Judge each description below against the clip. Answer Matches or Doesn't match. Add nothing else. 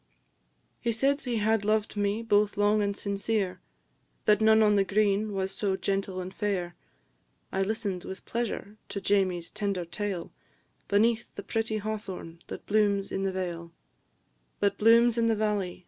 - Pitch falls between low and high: Doesn't match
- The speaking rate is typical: Matches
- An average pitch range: Doesn't match